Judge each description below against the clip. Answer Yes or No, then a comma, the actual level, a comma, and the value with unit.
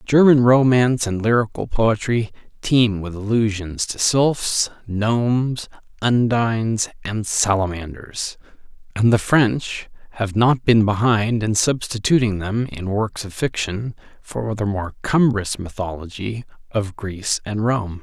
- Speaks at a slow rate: Yes, slow, 125 wpm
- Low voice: Yes, low, 110 Hz